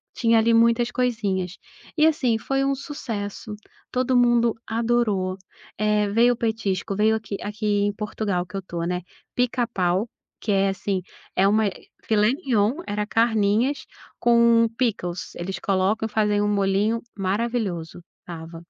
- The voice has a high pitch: Yes, high, 215 Hz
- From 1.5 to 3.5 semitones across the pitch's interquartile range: Yes, average, 3.2 semitones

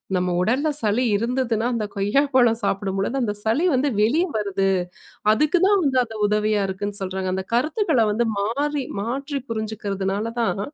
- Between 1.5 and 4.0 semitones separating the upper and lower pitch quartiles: No, average, 4.7 semitones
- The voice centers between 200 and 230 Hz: Yes, high, 220 Hz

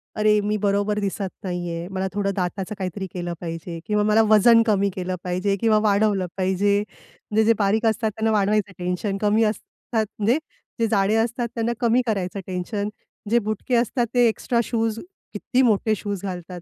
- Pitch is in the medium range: No, high, 205 Hz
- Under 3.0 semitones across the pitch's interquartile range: Yes, narrow, 2.6 semitones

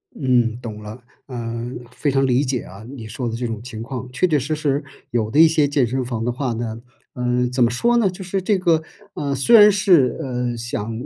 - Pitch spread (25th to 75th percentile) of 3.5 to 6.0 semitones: Yes, average, 4.0 semitones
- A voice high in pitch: No, low, 125 Hz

